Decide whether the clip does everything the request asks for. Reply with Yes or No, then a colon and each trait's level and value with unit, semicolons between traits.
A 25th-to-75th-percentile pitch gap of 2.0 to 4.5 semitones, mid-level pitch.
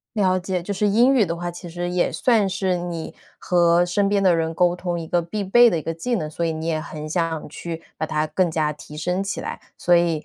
Yes: narrow, 2.6 semitones; medium, 175 Hz